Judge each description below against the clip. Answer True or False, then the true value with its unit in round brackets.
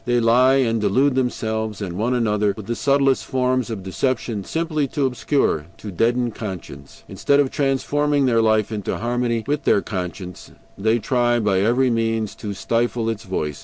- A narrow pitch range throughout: False (3.5 semitones)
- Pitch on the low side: True (115 Hz)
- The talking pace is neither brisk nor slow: True (170 wpm)